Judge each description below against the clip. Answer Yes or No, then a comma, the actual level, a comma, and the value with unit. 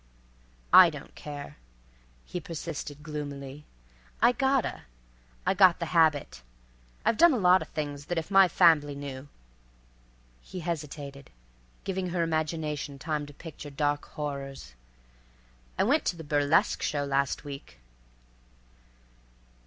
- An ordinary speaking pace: No, slow, 120 wpm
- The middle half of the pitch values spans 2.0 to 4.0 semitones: Yes, average, 3.4 semitones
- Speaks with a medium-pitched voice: Yes, medium, 145 Hz